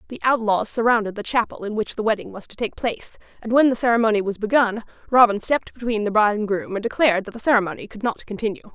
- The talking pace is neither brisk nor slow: No, fast, 235 wpm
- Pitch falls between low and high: No, high, 220 Hz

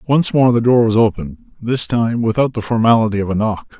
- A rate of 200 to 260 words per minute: Yes, fast, 205 wpm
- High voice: No, low, 115 Hz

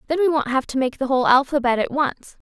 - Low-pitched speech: No, very high, 270 Hz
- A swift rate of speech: Yes, fast, 260 wpm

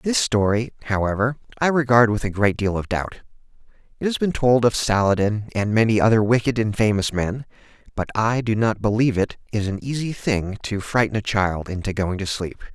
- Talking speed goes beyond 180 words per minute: Yes, average, 200 wpm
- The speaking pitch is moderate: No, low, 110 Hz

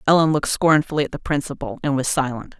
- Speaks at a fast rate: Yes, fast, 210 wpm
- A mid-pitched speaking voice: Yes, medium, 145 Hz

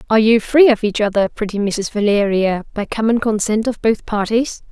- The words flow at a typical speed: Yes, average, 190 wpm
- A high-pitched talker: Yes, high, 215 Hz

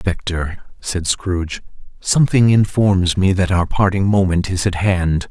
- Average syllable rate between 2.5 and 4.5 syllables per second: Yes, 4.2 syllables/s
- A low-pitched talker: Yes, very low, 95 Hz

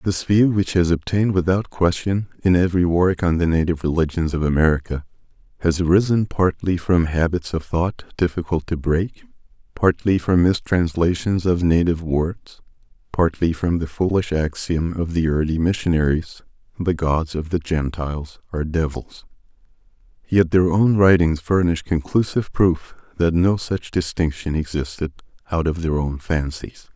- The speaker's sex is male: Yes, male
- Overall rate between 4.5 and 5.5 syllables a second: Yes, 4.9 syllables/s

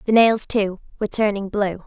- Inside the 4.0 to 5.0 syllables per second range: No, 5.2 syllables/s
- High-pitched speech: Yes, high, 210 Hz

